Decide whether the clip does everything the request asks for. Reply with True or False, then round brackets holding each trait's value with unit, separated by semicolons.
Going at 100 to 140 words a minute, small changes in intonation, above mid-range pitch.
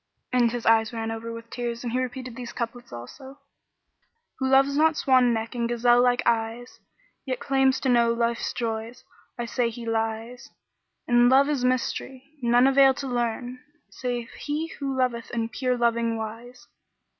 False (175 wpm; 1.9 semitones; 245 Hz)